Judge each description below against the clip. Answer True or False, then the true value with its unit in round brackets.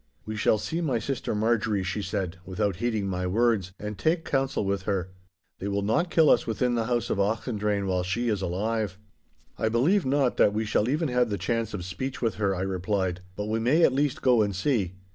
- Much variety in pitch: False (3.8 semitones)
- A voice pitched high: False (110 Hz)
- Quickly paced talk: True (220 wpm)